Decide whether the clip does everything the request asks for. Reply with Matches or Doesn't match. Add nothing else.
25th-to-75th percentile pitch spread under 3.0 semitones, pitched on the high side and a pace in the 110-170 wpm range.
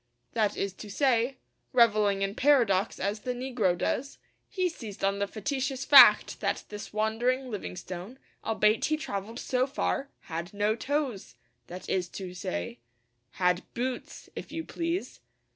Doesn't match